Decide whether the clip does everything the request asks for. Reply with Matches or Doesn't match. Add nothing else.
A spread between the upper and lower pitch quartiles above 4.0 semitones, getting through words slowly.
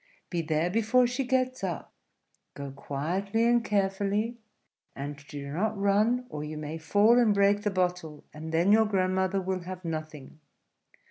Doesn't match